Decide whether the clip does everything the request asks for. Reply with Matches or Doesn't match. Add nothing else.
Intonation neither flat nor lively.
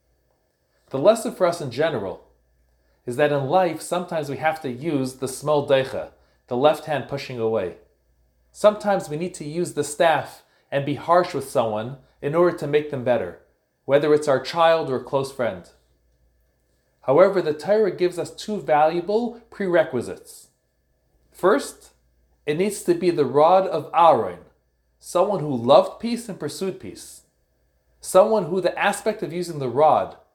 Doesn't match